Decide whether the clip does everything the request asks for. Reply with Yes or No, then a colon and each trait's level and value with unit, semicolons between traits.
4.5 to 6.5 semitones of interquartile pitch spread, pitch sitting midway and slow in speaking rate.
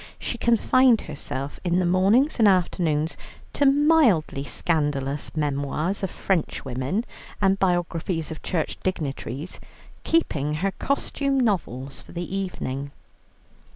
Yes: wide, 5.5 semitones; medium, 175 Hz; slow, 115 wpm